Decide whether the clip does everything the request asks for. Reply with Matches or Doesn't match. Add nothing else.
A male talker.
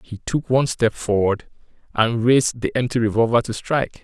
Matches